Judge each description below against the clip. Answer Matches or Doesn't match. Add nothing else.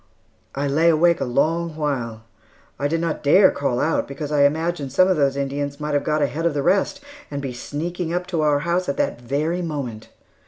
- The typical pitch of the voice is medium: Matches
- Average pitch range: Matches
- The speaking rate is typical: Doesn't match